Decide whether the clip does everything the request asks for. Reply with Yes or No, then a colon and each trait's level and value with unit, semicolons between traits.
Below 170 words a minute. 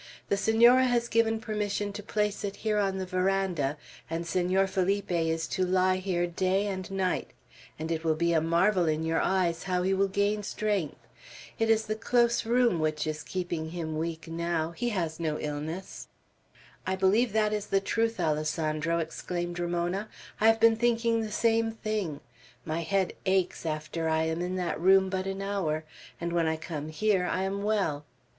No: average, 185 wpm